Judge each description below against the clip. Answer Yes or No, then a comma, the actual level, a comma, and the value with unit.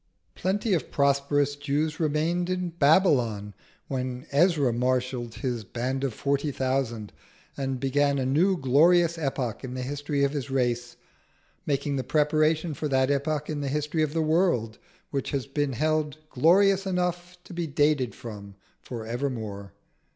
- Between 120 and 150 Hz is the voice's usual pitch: Yes, medium, 140 Hz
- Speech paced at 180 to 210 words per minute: No, average, 150 wpm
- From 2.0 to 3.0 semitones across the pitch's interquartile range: No, average, 3.5 semitones